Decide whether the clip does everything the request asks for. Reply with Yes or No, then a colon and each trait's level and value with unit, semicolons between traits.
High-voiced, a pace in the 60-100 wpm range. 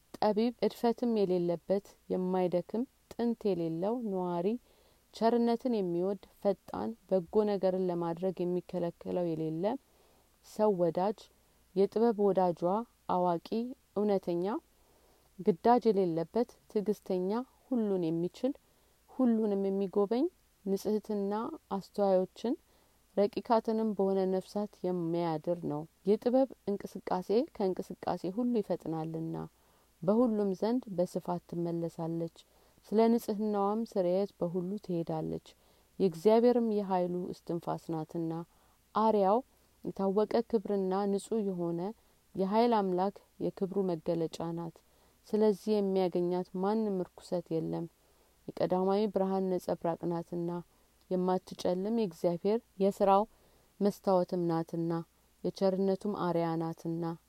Yes: high, 195 Hz; average, 80 wpm